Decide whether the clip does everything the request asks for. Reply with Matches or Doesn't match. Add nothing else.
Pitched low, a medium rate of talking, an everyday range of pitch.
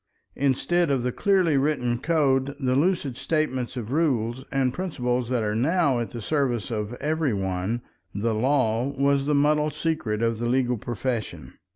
Matches